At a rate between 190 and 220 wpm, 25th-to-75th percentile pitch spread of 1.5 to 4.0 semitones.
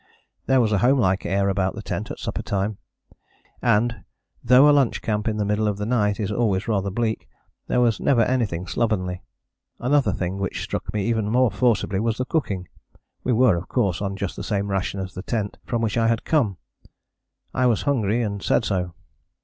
Yes: average, 200 wpm; average, 3.4 semitones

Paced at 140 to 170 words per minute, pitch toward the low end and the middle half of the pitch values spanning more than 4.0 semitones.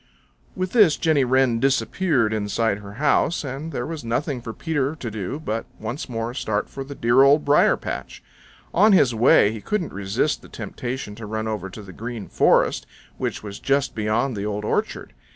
No: average, 190 wpm; low, 120 Hz; average, 4.8 semitones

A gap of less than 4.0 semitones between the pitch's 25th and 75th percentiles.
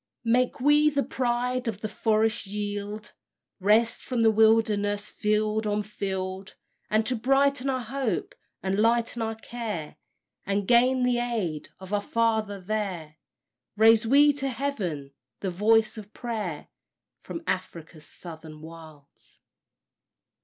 Yes: average, 3.6 semitones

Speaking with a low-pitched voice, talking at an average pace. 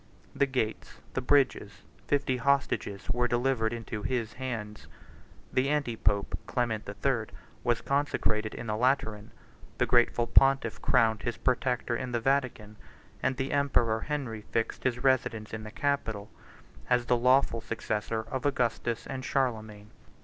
Yes: low, 120 Hz; average, 150 wpm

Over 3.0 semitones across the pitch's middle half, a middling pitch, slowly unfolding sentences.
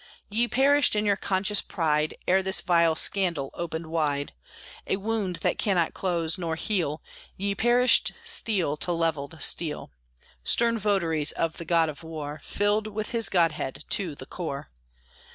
No: average, 4.4 semitones; medium, 175 Hz; average, 150 wpm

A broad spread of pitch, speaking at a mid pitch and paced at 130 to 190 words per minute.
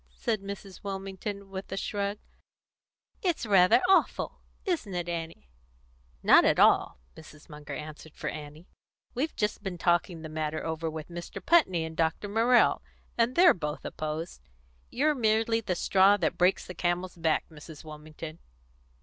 No: average, 4.4 semitones; medium, 180 Hz; average, 150 wpm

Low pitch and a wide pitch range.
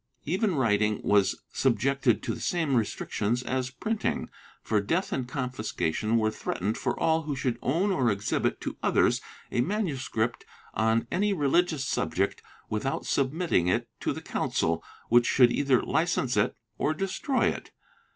Yes: low, 130 Hz; wide, 6.6 semitones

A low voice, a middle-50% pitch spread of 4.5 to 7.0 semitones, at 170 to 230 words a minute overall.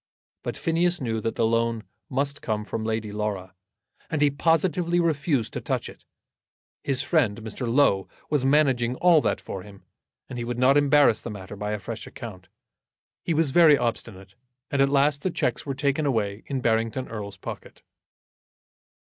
Yes: low, 125 Hz; average, 5.0 semitones; average, 175 wpm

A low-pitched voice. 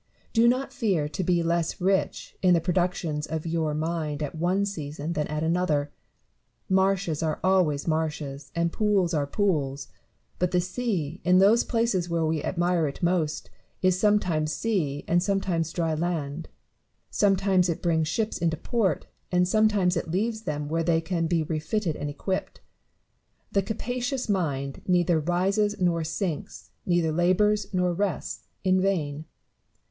No: medium, 175 Hz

